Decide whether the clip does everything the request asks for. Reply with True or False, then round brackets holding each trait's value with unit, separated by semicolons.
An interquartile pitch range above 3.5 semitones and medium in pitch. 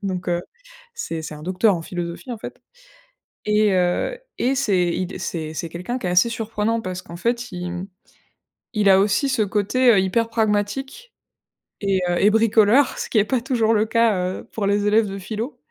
False (3.9 semitones; 210 Hz)